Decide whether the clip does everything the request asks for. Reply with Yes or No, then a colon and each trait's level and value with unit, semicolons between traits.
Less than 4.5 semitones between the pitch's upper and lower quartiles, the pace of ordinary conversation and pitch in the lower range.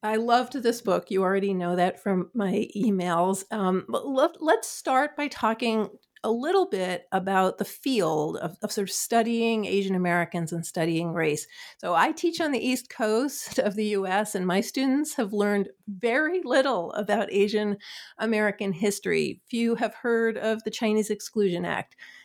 No: average, 3.5 semitones; average, 165 wpm; high, 210 Hz